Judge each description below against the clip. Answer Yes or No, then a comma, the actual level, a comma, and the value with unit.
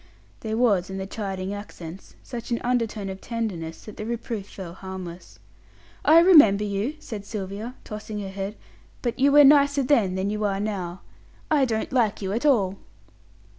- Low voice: No, high, 210 Hz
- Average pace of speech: Yes, average, 170 wpm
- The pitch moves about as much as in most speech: Yes, average, 3.6 semitones